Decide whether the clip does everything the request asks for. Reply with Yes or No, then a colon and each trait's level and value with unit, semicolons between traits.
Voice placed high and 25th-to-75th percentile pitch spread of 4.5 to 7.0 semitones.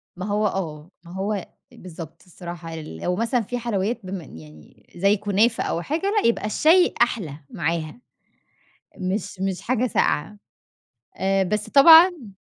Yes: high, 195 Hz; average, 5.2 semitones